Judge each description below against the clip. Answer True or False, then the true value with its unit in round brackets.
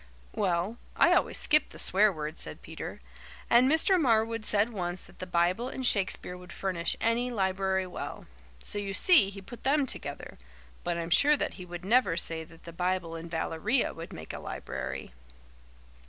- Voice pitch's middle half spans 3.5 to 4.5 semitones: False (5.2 semitones)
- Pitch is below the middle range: False (190 Hz)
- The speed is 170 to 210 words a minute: True (180 wpm)